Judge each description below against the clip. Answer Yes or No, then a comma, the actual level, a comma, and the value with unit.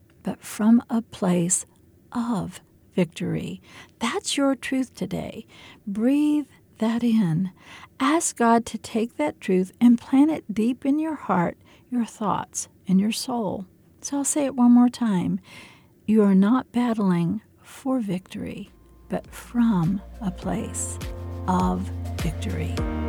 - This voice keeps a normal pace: No, slow, 130 wpm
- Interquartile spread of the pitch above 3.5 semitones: Yes, average, 5.2 semitones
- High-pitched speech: Yes, high, 220 Hz